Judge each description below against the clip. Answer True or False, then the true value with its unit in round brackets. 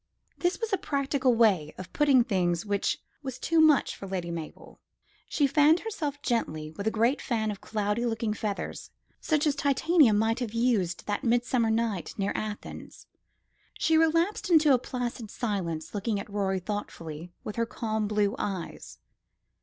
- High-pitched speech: True (225 Hz)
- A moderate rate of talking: True (160 wpm)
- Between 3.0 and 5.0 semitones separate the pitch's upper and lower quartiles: False (5.6 semitones)